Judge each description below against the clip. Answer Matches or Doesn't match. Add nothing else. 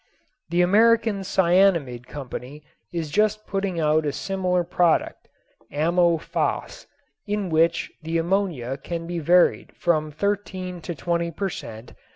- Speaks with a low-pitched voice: Doesn't match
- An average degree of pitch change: Matches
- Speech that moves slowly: Matches